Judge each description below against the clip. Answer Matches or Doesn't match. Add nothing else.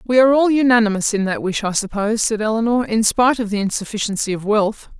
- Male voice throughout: Doesn't match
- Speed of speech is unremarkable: Doesn't match